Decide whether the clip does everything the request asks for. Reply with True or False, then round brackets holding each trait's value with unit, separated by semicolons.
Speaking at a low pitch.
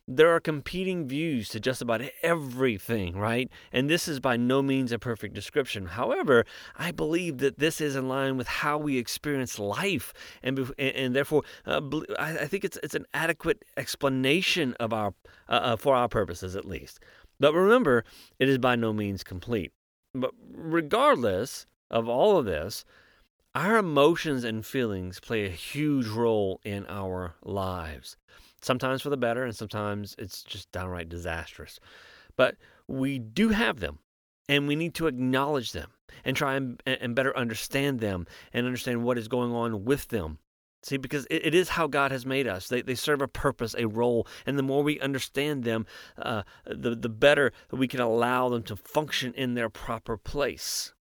True (125 Hz)